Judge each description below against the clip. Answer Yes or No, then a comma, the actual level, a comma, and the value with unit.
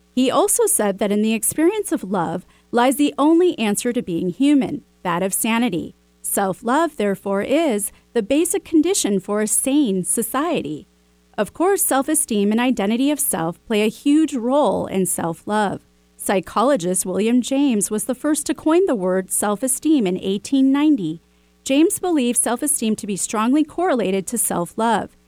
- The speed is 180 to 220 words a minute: No, average, 165 wpm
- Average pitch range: No, wide, 7.0 semitones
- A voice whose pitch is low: No, high, 230 Hz